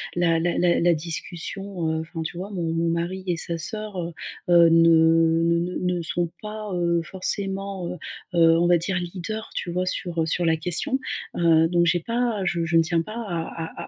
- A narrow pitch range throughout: Yes, narrow, 2.0 semitones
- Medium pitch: Yes, medium, 175 Hz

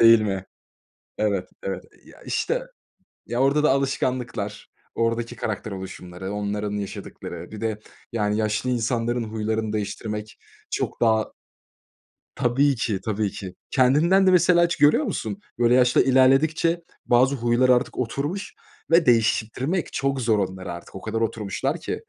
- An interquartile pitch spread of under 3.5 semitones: No, average, 4.2 semitones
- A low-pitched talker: Yes, low, 115 Hz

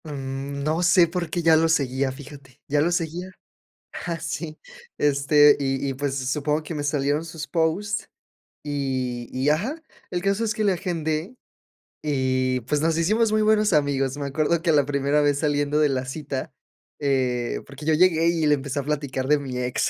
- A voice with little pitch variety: No, average, 3.2 semitones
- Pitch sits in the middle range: Yes, medium, 150 Hz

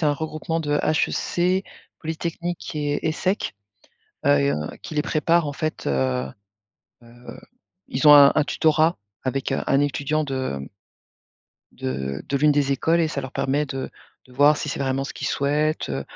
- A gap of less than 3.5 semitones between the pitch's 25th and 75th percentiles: Yes, average, 2.8 semitones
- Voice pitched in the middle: Yes, medium, 145 Hz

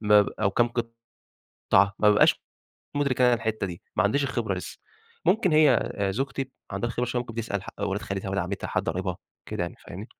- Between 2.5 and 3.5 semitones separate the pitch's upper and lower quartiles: No, average, 4.1 semitones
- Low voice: Yes, low, 105 Hz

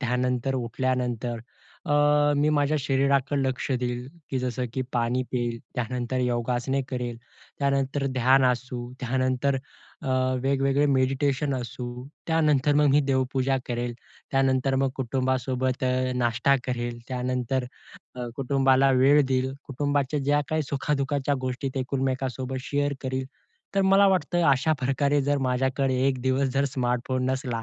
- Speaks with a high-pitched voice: No, low, 130 Hz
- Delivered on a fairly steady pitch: Yes, narrow, 1.7 semitones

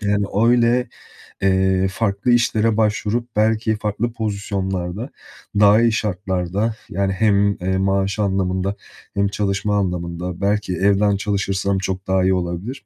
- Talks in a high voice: No, low, 100 Hz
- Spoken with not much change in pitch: Yes, narrow, 2.1 semitones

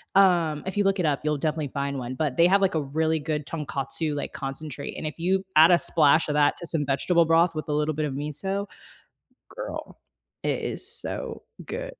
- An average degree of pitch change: Yes, average, 3.0 semitones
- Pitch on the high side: No, medium, 155 Hz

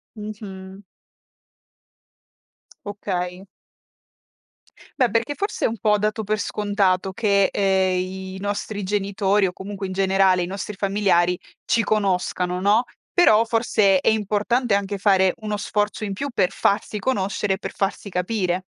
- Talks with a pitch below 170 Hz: No, high, 200 Hz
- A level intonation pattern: Yes, narrow, 1.8 semitones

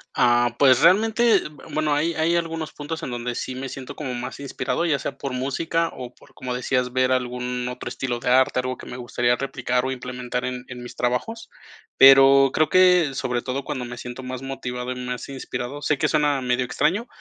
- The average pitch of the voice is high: No, low, 130 Hz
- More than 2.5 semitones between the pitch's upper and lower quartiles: Yes, average, 2.9 semitones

